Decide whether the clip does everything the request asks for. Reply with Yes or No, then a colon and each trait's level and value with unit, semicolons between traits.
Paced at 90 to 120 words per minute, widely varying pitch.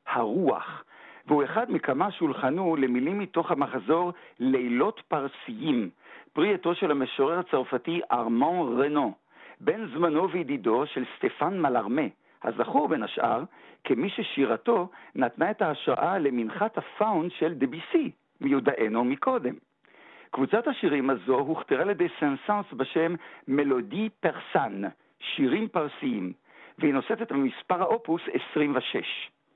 Yes: average, 115 wpm; wide, 6.8 semitones